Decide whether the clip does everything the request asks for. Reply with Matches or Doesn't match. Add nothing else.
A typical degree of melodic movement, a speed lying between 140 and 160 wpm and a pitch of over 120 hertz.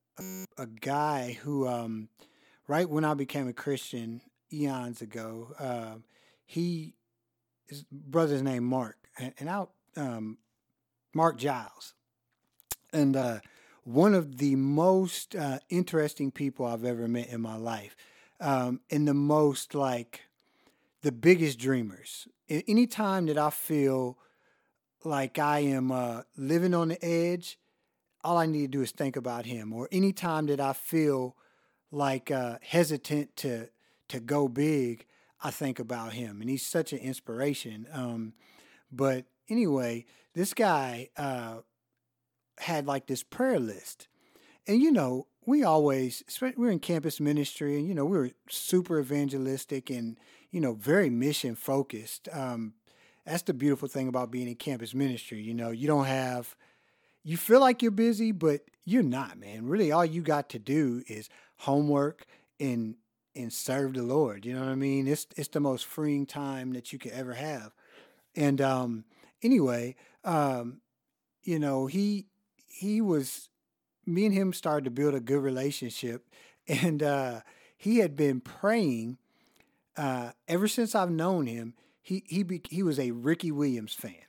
Matches